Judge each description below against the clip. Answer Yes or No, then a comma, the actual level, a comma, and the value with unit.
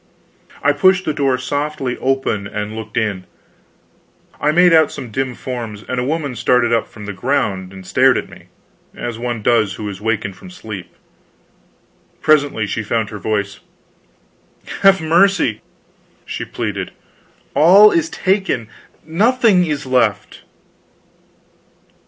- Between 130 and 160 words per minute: Yes, slow, 135 wpm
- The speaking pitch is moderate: No, low, 125 Hz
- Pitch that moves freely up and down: Yes, wide, 6.7 semitones